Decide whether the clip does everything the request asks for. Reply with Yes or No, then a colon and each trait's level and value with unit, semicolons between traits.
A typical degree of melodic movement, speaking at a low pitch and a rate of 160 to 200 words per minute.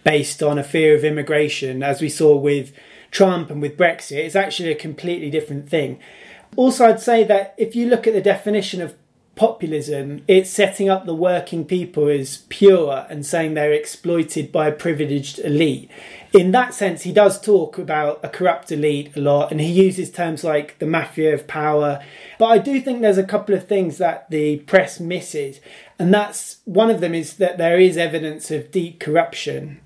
No: average, 4.4 semitones; medium, 165 Hz; average, 190 wpm